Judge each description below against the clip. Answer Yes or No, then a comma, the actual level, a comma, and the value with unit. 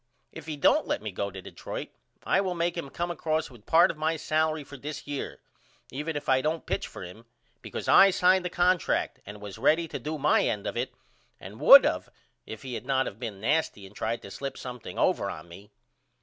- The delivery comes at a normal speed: No, fast, 225 wpm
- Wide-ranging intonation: Yes, wide, 6.2 semitones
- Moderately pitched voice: Yes, medium, 145 Hz